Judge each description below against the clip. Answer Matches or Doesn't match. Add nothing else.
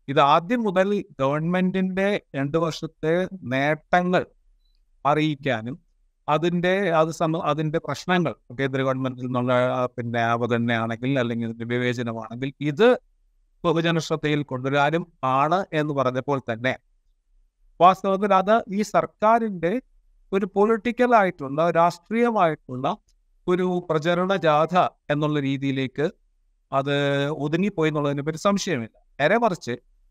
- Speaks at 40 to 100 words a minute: Matches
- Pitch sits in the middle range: Matches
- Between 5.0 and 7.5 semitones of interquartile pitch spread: Matches